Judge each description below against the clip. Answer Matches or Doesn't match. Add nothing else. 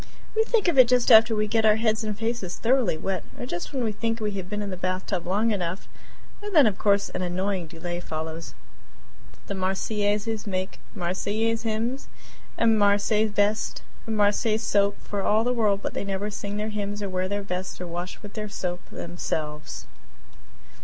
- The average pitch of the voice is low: Doesn't match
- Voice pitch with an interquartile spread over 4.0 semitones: Doesn't match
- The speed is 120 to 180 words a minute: Doesn't match